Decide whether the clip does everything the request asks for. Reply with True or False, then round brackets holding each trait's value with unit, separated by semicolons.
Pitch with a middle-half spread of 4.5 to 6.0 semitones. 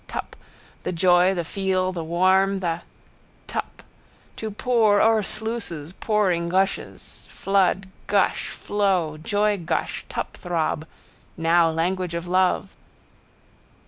False (2.8 semitones)